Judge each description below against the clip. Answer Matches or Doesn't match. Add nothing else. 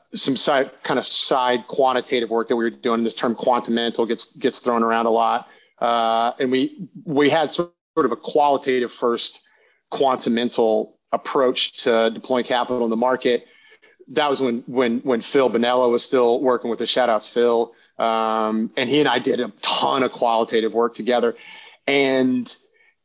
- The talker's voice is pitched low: Matches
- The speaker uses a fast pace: Doesn't match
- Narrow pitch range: Matches